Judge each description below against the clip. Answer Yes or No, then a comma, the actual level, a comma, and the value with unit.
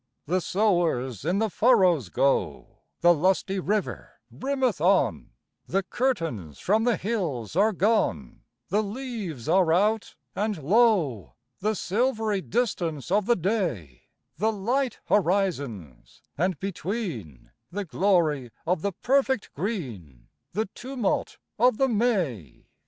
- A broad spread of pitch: Yes, wide, 6.2 semitones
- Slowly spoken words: Yes, slow, 120 wpm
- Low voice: No, high, 190 Hz